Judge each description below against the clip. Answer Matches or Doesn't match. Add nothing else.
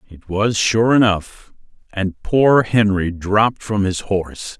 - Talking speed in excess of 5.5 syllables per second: Doesn't match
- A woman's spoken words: Doesn't match